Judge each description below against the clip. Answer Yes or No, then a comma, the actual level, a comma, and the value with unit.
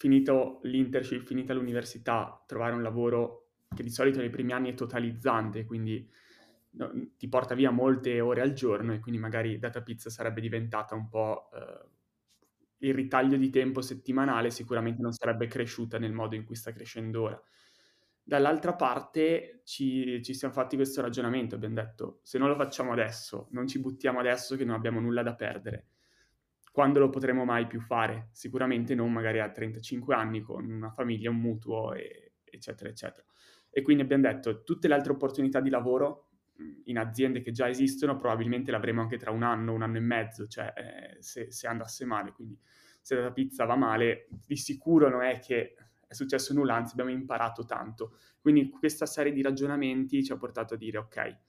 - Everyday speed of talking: No, fast, 180 wpm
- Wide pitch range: No, average, 2.7 semitones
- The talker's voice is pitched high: No, low, 120 Hz